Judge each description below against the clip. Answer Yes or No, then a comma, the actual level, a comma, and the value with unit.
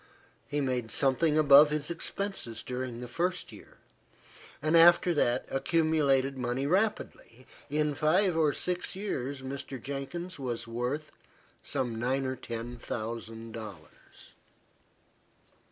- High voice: No, low, 135 Hz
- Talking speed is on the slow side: Yes, slow, 120 wpm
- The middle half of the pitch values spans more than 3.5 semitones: Yes, average, 4.3 semitones